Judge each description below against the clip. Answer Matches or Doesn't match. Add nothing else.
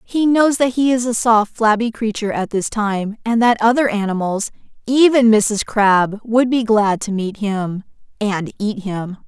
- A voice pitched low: Doesn't match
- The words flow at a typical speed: Matches